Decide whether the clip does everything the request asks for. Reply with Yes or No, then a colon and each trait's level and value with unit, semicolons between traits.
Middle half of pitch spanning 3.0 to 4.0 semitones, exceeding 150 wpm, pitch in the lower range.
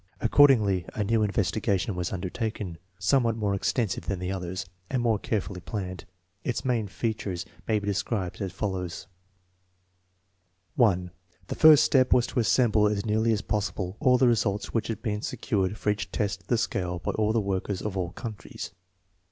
Yes: average, 3.3 semitones; average, 175 wpm; low, 105 Hz